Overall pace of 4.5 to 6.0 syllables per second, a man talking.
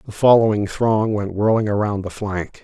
Yes: 4.8 syllables/s; male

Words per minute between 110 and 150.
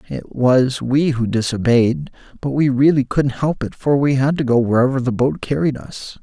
No: average, 200 wpm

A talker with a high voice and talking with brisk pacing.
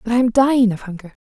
Yes: high, 230 Hz; fast, 290 wpm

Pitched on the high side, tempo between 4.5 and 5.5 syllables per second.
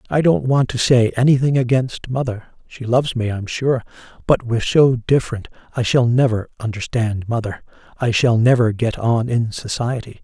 No: low, 120 Hz; 5.1 syllables/s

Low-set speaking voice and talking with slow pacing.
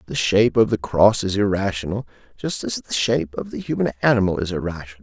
No: low, 100 Hz; fast, 205 wpm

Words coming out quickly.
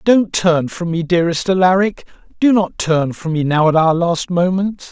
No: average, 195 wpm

